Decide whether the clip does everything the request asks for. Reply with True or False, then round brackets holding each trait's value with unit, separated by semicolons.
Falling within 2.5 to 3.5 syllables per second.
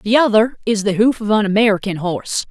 False (5.9 syllables/s)